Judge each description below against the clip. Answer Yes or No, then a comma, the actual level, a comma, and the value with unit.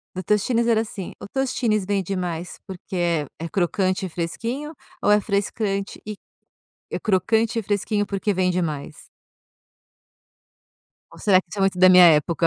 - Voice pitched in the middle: No, high, 195 Hz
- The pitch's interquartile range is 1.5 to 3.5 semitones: Yes, average, 2.9 semitones